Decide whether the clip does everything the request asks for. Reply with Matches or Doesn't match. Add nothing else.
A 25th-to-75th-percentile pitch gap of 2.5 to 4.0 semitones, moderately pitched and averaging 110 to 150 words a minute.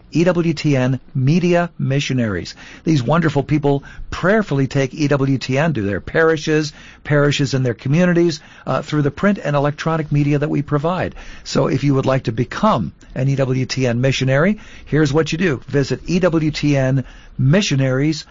Matches